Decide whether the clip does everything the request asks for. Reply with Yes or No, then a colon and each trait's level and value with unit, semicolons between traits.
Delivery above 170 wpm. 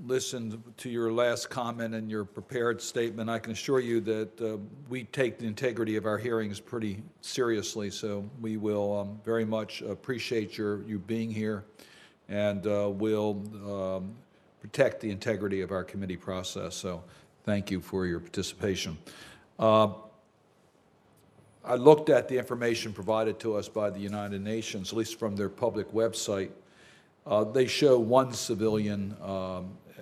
No: average, 155 wpm